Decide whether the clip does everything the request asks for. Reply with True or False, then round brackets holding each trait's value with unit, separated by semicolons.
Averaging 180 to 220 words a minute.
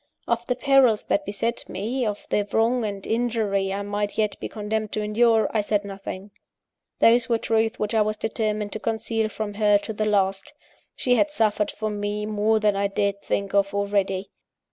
True (190 wpm)